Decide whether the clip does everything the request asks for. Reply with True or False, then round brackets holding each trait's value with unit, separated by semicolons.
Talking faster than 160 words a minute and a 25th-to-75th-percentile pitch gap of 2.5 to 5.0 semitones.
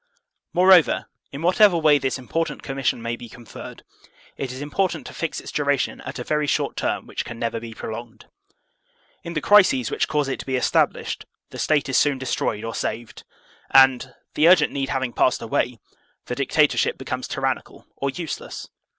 True (175 wpm; 4.1 semitones)